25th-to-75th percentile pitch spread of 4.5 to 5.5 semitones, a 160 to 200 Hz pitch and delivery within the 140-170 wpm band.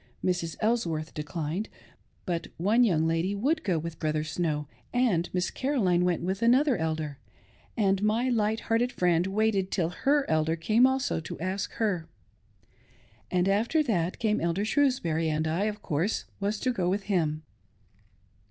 Yes: average, 5.2 semitones; medium, 185 Hz; average, 155 wpm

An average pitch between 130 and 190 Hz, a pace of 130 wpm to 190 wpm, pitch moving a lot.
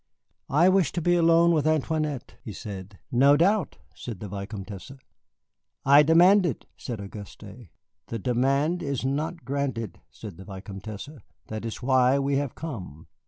Yes: low, 135 Hz; average, 150 wpm; wide, 6.7 semitones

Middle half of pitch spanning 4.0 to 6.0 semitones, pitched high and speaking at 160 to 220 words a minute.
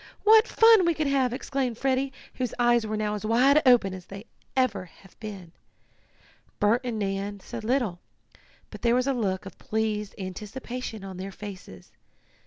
Yes: average, 4.5 semitones; high, 220 Hz; average, 170 wpm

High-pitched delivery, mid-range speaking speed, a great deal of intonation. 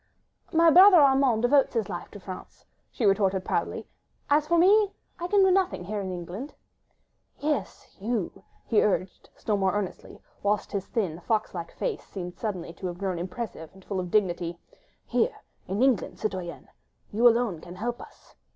Yes: high, 210 Hz; average, 180 wpm; wide, 6.8 semitones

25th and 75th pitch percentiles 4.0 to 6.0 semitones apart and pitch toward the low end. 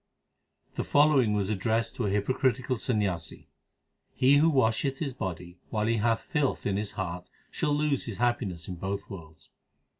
Yes: average, 5.3 semitones; low, 110 Hz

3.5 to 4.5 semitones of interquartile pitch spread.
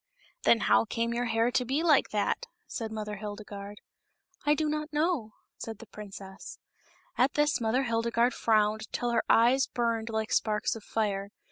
No: average, 2.8 semitones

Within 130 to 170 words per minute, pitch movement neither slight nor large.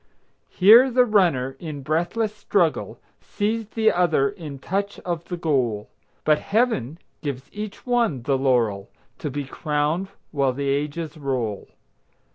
No: slow, 135 wpm; wide, 6.8 semitones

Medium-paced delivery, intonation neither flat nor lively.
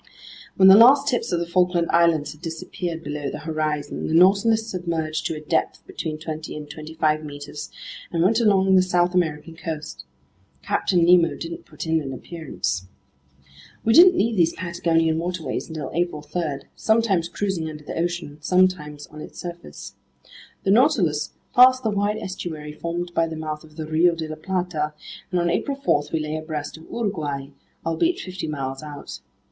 Yes: average, 175 wpm; average, 3.1 semitones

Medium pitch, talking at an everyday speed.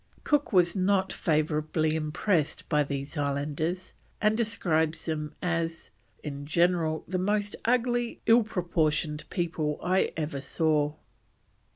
No: medium, 165 Hz; slow, 115 wpm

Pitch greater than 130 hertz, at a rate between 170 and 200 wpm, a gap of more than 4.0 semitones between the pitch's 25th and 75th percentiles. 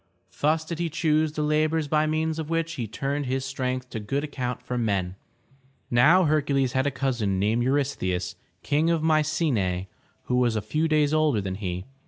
Yes: medium, 140 Hz; average, 195 wpm; average, 4.6 semitones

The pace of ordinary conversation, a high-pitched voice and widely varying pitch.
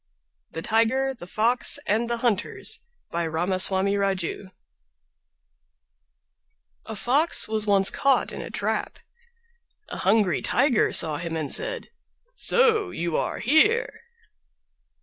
No: slow, 115 wpm; high, 220 Hz; wide, 6.3 semitones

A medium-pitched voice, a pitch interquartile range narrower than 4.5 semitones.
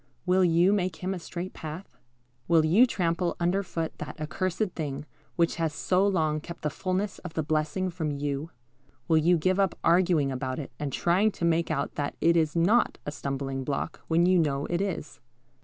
Yes: medium, 165 Hz; average, 3.2 semitones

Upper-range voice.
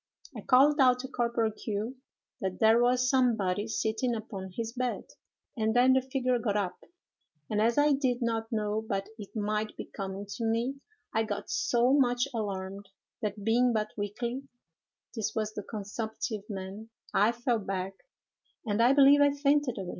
Yes: high, 225 Hz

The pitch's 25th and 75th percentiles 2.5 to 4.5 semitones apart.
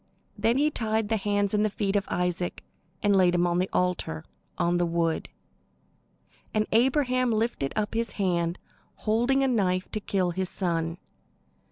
Yes: average, 4.0 semitones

